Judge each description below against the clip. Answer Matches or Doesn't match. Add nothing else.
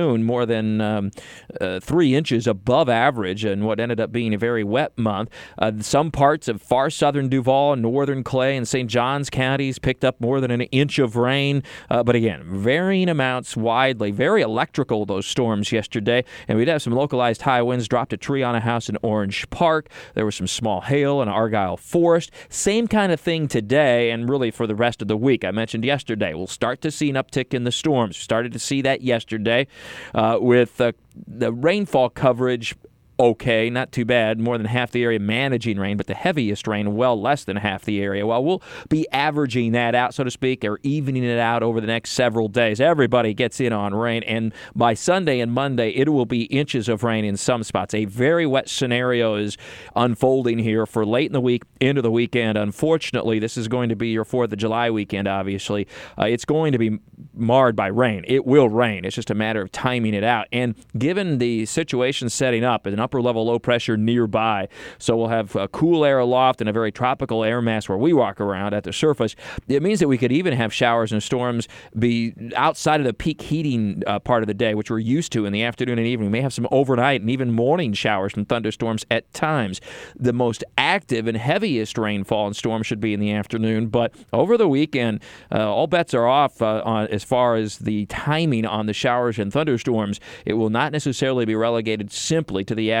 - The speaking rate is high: Matches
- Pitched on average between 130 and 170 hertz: Doesn't match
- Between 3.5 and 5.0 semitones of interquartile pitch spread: Doesn't match